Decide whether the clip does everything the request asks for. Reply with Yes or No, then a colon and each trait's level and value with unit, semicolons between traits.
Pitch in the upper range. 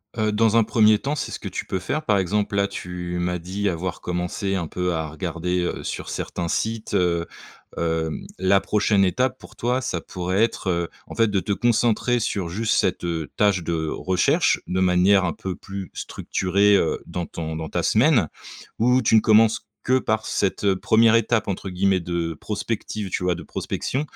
No: very low, 95 Hz